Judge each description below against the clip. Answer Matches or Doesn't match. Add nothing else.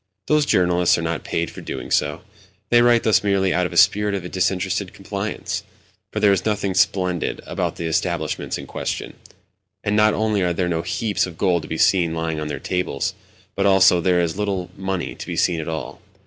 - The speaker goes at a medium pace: Doesn't match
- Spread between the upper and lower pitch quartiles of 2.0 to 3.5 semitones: Matches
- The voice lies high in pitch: Doesn't match